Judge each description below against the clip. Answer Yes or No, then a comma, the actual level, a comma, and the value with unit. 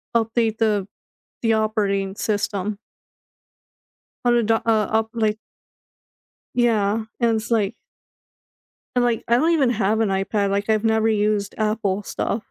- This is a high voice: Yes, high, 220 Hz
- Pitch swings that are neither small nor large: No, narrow, 1.8 semitones